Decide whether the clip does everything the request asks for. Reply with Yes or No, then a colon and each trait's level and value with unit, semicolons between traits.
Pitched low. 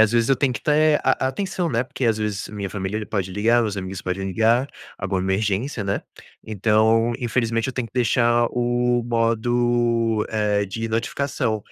Yes: low, 115 Hz